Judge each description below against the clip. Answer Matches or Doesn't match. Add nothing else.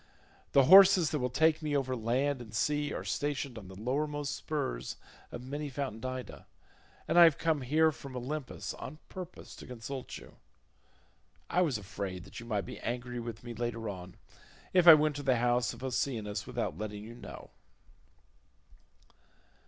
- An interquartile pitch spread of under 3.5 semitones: Doesn't match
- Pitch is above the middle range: Doesn't match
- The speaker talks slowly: Doesn't match